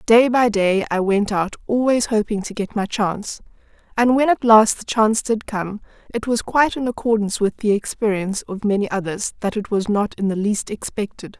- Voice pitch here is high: Yes, high, 215 Hz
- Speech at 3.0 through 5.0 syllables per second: No, 5.3 syllables/s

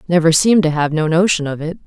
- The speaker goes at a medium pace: No, fast, 260 wpm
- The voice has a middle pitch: Yes, medium, 165 Hz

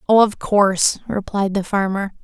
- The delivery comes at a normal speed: Yes, average, 160 wpm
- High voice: Yes, high, 200 Hz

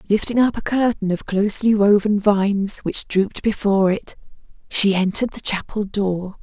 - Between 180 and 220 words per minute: No, average, 160 wpm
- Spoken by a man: No, female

